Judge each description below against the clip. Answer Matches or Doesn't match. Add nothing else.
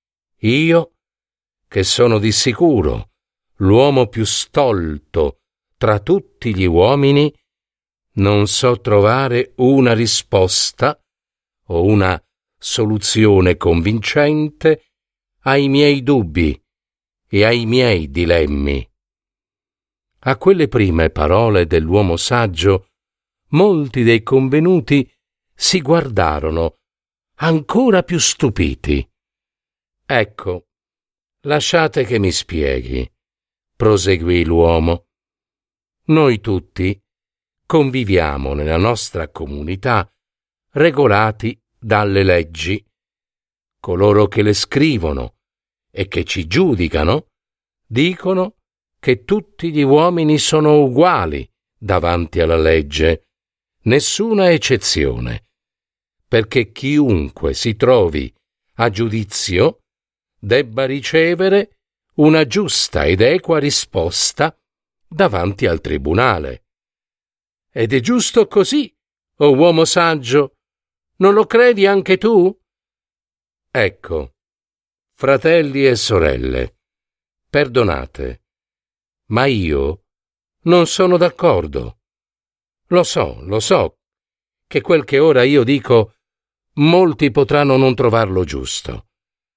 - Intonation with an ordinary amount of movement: Doesn't match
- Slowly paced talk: Matches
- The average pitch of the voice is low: Matches